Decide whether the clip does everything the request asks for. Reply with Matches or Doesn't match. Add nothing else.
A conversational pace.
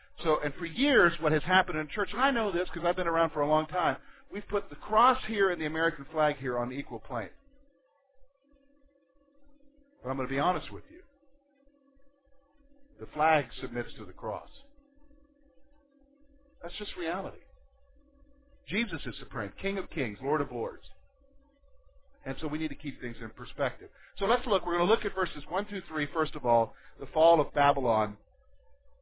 Matches